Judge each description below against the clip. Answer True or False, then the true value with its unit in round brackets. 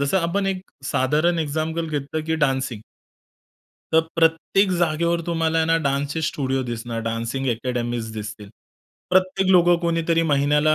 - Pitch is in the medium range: True (155 Hz)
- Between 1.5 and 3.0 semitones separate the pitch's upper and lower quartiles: False (4.1 semitones)